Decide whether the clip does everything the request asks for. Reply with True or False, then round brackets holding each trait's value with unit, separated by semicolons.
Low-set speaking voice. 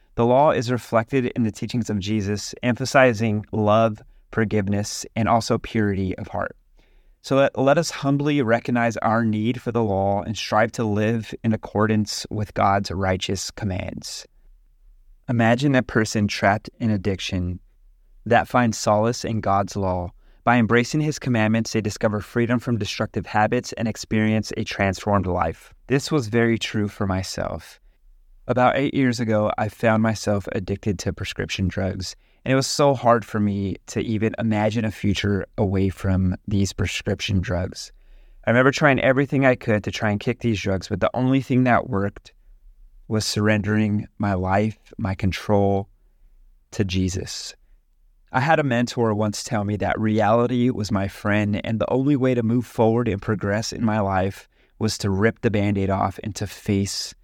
True (110 Hz)